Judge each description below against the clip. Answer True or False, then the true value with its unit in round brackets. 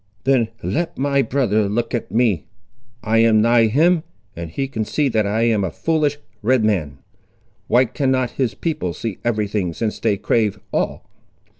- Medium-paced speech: True (170 wpm)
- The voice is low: True (115 Hz)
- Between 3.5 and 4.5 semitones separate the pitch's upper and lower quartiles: True (4.2 semitones)